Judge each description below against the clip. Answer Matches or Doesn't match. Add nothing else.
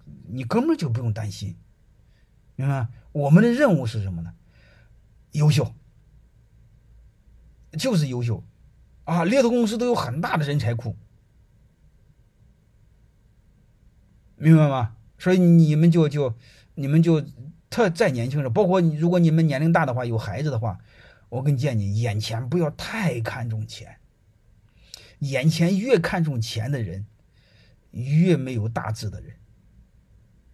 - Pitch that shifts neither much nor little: Doesn't match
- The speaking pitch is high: Doesn't match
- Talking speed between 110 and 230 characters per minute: Matches